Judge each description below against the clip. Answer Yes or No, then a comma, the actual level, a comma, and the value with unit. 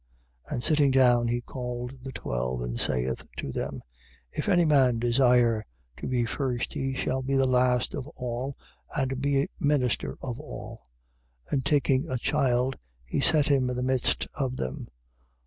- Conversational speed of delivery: Yes, average, 170 wpm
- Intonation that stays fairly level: Yes, narrow, 2.1 semitones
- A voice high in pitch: No, low, 130 Hz